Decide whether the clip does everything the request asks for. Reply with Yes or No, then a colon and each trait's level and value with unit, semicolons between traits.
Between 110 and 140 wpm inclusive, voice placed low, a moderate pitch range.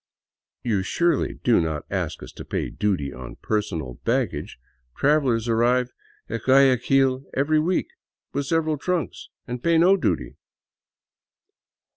No: slow, 135 wpm; low, 125 Hz; wide, 6.2 semitones